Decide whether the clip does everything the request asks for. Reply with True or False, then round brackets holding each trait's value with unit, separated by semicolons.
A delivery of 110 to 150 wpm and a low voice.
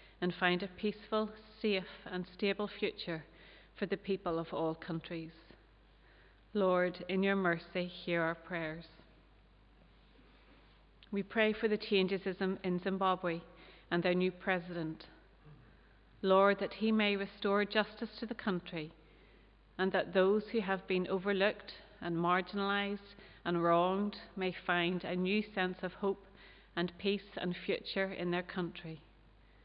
False (135 wpm; 185 Hz)